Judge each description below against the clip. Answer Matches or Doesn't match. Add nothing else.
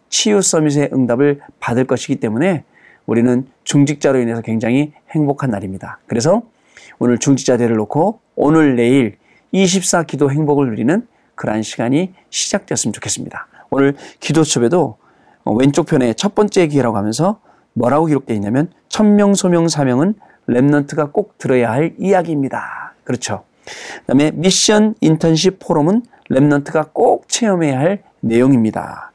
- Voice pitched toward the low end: Doesn't match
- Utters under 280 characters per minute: Doesn't match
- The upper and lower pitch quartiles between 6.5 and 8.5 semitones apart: Doesn't match